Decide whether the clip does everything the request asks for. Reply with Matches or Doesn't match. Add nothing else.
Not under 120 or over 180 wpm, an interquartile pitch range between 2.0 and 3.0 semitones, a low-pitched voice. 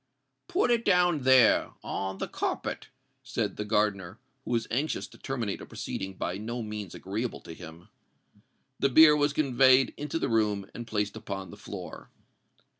Doesn't match